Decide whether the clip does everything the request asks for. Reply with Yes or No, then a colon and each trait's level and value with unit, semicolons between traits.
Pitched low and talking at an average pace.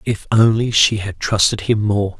Yes: low, 105 Hz; average, 190 wpm